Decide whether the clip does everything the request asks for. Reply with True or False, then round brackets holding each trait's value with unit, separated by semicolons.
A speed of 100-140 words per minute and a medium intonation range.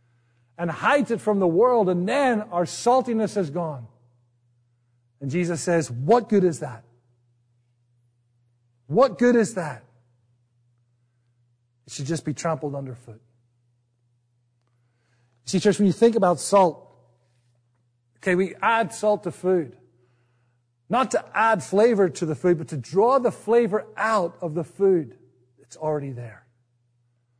False (135 wpm; 7.6 semitones)